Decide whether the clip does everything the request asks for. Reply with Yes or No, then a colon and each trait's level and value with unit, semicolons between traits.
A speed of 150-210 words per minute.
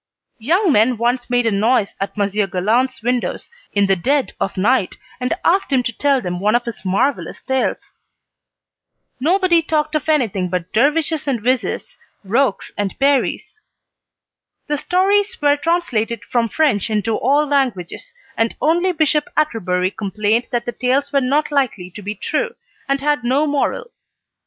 Yes: average, 155 wpm